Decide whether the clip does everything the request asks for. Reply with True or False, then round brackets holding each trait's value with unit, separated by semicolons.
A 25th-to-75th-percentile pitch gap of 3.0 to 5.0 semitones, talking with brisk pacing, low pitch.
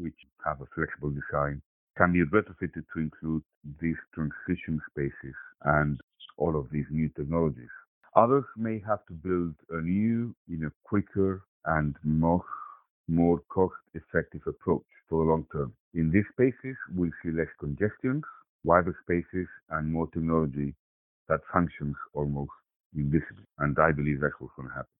False (3.5 semitones; 145 wpm; 80 Hz)